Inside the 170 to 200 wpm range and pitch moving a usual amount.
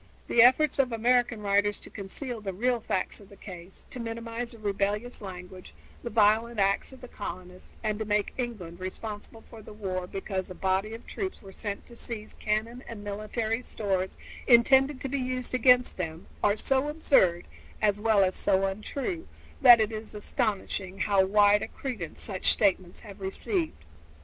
Yes: average, 175 wpm; average, 3.5 semitones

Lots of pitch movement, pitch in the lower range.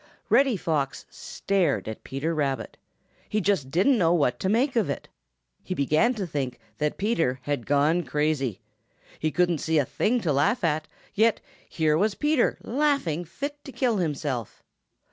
No: wide, 7.1 semitones; medium, 165 Hz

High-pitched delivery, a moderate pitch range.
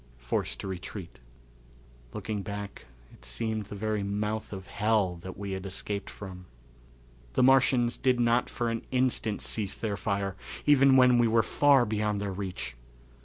No: low, 105 Hz; average, 3.2 semitones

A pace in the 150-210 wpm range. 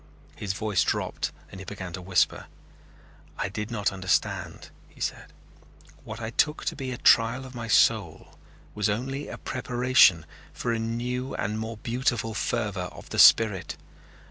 Yes: average, 160 wpm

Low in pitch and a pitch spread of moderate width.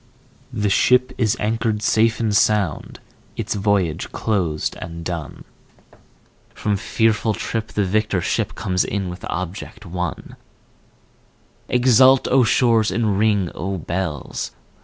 Yes: low, 105 Hz; average, 3.5 semitones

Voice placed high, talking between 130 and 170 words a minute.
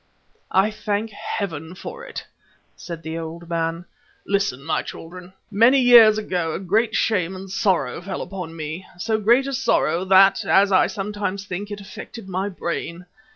Yes: high, 195 Hz; average, 160 wpm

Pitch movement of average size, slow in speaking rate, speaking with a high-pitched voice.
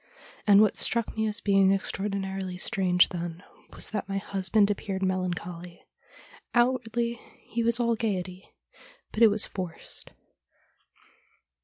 Yes: average, 3.0 semitones; slow, 130 wpm; high, 195 Hz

